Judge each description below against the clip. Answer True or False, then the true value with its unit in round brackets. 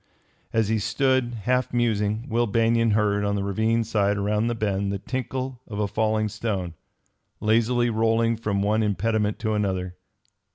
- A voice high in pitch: False (110 Hz)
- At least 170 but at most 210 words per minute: False (160 wpm)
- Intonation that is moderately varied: False (2.2 semitones)